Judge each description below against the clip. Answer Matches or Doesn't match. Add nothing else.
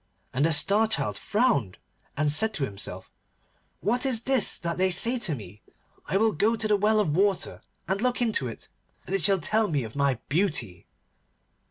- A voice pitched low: Doesn't match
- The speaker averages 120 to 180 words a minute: Doesn't match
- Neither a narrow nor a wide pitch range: Doesn't match